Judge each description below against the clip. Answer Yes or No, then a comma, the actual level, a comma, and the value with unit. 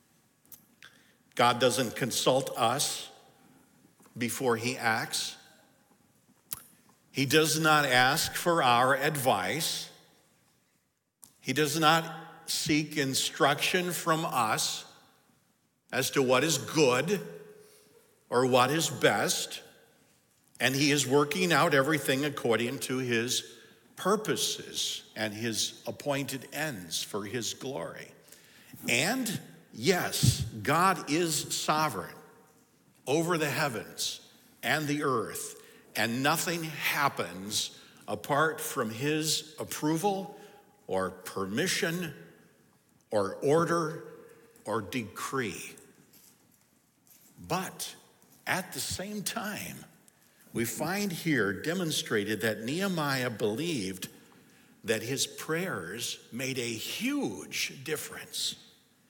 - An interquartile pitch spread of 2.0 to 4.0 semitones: No, average, 5.1 semitones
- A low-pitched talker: No, medium, 150 Hz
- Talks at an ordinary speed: No, slow, 90 wpm